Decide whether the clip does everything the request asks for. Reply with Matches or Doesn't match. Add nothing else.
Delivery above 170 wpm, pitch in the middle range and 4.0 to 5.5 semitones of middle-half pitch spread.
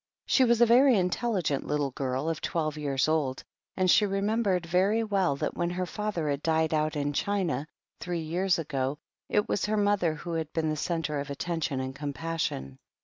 Matches